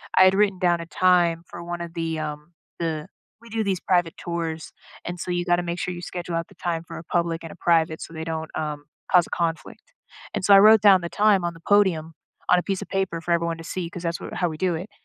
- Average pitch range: No, narrow, 1.8 semitones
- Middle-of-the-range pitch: Yes, medium, 170 Hz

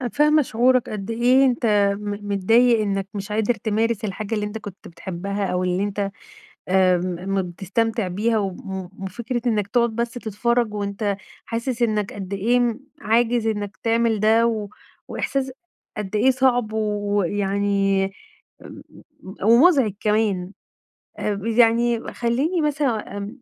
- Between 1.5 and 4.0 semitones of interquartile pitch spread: Yes, average, 3.0 semitones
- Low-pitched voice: No, high, 215 Hz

